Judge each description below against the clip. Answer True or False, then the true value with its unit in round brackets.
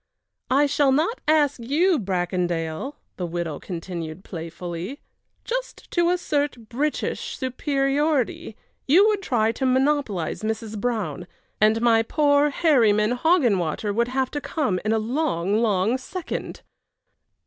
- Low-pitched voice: False (240 Hz)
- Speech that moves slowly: True (125 wpm)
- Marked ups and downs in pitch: True (6.7 semitones)